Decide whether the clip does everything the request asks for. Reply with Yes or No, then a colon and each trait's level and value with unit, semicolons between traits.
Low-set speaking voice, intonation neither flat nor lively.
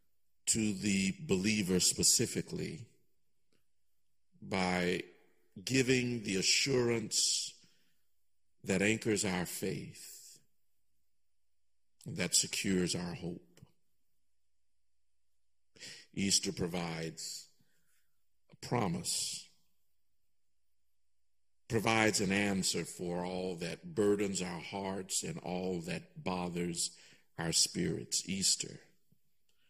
No: very low, 90 Hz; wide, 6.6 semitones